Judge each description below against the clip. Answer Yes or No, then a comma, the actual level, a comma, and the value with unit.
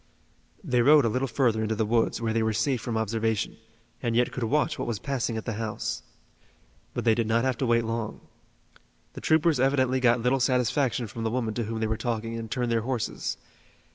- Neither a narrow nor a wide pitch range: No, narrow, 2.3 semitones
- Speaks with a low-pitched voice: Yes, low, 115 Hz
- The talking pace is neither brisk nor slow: No, fast, 215 wpm